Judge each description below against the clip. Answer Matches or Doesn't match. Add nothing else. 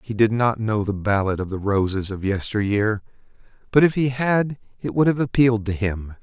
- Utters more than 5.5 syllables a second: Doesn't match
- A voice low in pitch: Matches